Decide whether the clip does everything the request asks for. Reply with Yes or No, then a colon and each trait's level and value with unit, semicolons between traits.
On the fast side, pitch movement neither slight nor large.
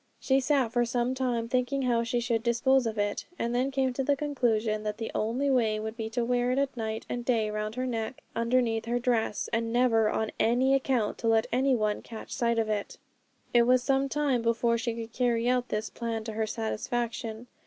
No: fast, 215 wpm; narrow, 2.2 semitones